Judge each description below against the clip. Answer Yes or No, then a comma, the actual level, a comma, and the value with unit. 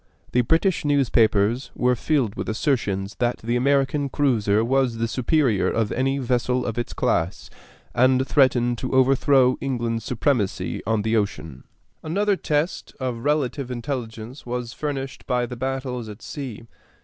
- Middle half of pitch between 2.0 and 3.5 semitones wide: Yes, average, 3.0 semitones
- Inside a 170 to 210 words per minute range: No, average, 145 wpm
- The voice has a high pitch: No, low, 125 Hz